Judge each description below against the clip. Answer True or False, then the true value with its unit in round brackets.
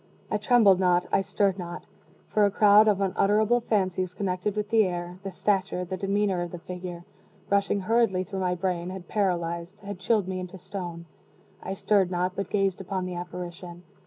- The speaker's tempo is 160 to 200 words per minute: True (185 wpm)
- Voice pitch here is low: False (185 Hz)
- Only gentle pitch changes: True (2.1 semitones)